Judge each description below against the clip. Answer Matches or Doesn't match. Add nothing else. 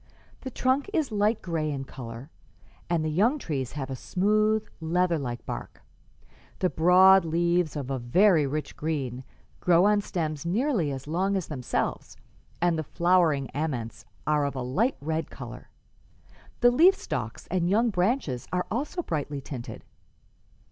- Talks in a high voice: Doesn't match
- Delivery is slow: Doesn't match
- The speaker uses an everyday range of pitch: Doesn't match